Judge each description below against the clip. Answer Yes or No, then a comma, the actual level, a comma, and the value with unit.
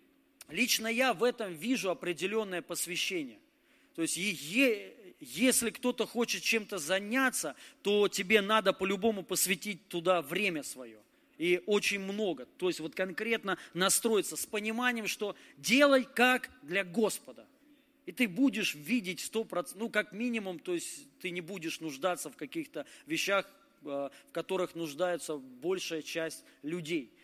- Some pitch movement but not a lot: No, wide, 5.8 semitones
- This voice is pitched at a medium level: No, high, 200 Hz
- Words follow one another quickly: No, average, 135 wpm